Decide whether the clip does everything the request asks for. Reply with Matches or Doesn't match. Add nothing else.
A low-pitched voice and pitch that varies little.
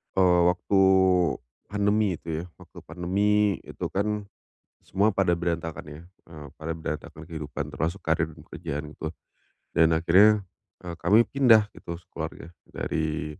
Doesn't match